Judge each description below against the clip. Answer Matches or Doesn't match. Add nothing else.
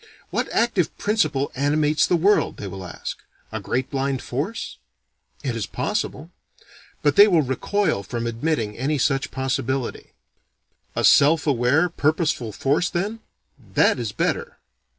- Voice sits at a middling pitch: Matches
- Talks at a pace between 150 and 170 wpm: Doesn't match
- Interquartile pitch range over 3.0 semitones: Matches